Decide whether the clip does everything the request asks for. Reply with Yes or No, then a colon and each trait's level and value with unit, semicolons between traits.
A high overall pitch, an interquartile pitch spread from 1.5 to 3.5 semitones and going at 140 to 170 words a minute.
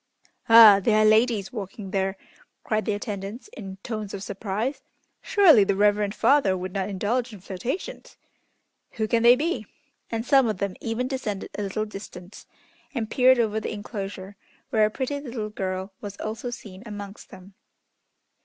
Yes: high, 210 Hz; average, 3.1 semitones; average, 165 wpm